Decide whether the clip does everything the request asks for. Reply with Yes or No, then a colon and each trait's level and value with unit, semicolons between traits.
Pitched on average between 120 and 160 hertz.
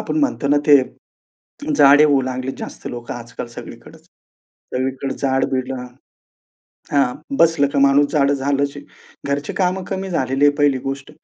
Yes: medium, 140 Hz